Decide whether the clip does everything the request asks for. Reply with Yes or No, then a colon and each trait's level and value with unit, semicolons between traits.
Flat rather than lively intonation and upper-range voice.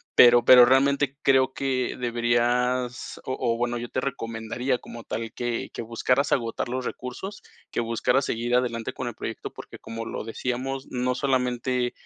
No: narrow, 1.6 semitones; low, 125 Hz